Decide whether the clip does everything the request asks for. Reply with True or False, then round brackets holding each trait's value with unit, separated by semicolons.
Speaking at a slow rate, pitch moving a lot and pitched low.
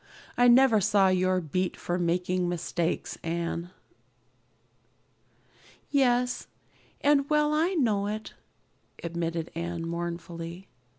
False (100 wpm; 6.2 semitones; 185 Hz)